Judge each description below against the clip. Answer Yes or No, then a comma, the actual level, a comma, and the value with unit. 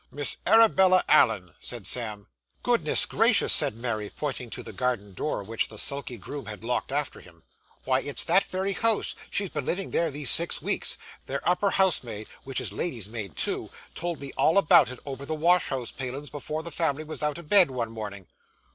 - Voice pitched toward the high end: No, medium, 140 Hz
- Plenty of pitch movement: Yes, wide, 6.6 semitones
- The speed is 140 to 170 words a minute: No, average, 200 wpm